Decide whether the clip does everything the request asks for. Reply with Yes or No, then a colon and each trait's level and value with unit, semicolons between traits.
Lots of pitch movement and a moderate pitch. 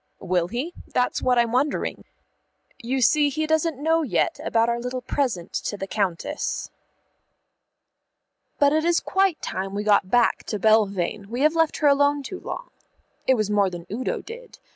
No: wide, 6.5 semitones; very high, 250 Hz